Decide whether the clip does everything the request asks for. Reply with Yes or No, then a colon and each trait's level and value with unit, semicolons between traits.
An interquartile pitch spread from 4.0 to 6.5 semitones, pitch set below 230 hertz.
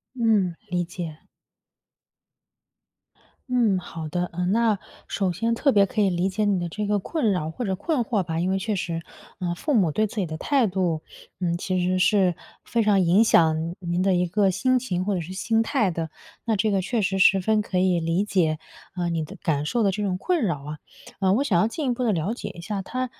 No: average, 3.6 semitones; high, 190 Hz